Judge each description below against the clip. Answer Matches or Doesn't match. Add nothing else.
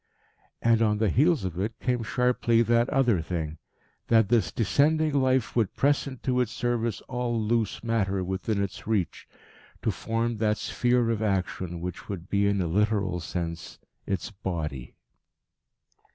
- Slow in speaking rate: Doesn't match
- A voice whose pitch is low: Matches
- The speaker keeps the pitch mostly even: Doesn't match